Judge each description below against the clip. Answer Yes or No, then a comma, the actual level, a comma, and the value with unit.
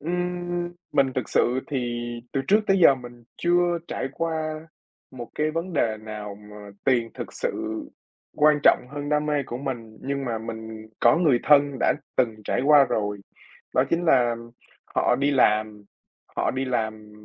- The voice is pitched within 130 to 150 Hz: Yes, low, 135 Hz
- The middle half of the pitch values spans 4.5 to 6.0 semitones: Yes, average, 5.3 semitones